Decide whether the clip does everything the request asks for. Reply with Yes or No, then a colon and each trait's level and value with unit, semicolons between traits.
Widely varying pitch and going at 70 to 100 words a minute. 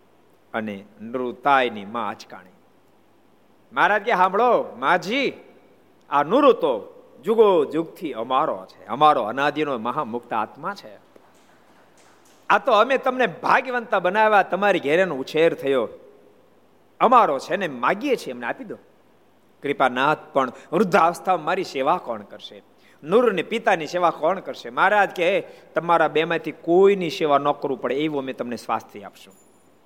No: wide, 7.9 semitones; average, 135 wpm